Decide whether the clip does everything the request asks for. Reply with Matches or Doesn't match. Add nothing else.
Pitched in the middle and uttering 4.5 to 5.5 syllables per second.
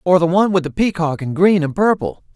Doesn't match